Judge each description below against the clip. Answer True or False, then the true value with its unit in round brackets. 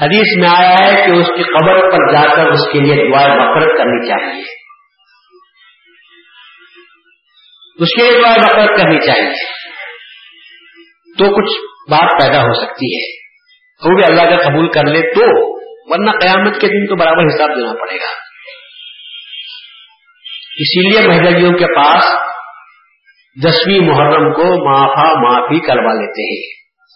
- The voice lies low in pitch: False (190 Hz)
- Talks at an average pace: True (140 wpm)